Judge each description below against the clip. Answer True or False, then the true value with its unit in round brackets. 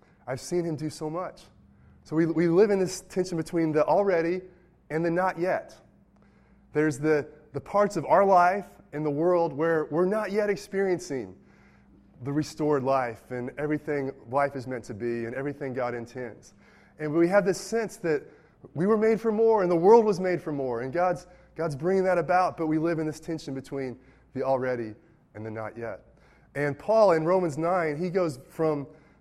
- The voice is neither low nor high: True (160 Hz)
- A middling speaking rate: True (195 wpm)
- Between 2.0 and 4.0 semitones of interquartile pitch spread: False (4.7 semitones)